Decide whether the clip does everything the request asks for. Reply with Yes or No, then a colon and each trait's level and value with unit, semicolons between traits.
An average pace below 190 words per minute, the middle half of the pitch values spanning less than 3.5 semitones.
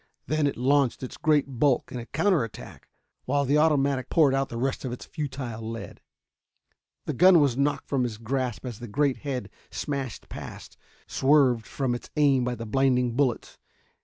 Yes: average, 180 wpm; average, 2.8 semitones